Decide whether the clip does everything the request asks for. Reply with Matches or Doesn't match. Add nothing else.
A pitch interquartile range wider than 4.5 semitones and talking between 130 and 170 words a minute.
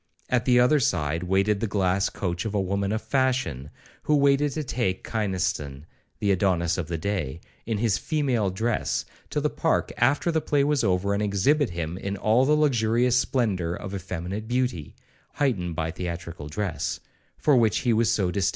Doesn't match